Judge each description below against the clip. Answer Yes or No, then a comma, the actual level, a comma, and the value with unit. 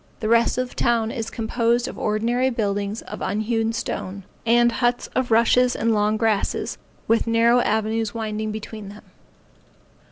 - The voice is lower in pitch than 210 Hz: No, high, 225 Hz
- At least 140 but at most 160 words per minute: Yes, average, 155 wpm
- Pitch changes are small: Yes, narrow, 1.7 semitones